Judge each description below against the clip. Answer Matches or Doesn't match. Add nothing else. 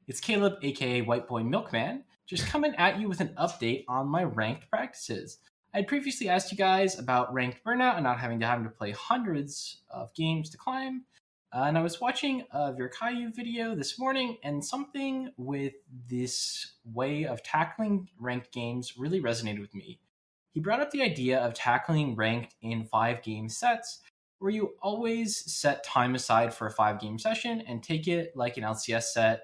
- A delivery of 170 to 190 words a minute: Matches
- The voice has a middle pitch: Matches